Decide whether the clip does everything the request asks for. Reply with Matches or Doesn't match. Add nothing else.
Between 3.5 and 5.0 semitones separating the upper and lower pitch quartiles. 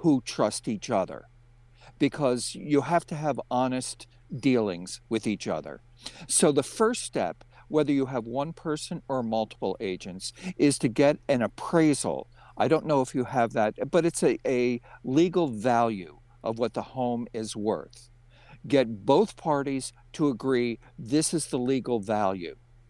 Matches